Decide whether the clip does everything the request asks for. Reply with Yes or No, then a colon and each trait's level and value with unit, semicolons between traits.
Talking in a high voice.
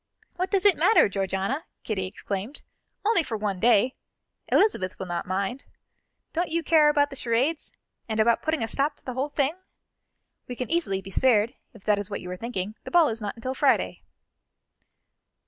Yes: high, 235 Hz